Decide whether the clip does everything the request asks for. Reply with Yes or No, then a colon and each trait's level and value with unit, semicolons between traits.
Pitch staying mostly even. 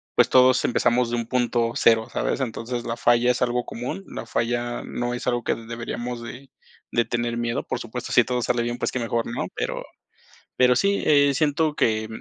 Yes: narrow, 1.2 semitones